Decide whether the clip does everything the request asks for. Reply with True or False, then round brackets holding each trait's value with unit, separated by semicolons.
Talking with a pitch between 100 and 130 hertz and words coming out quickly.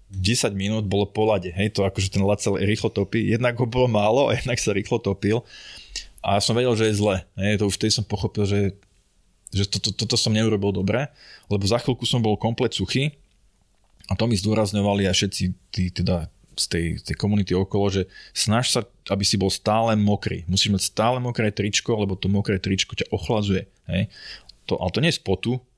True (105 Hz; 205 wpm)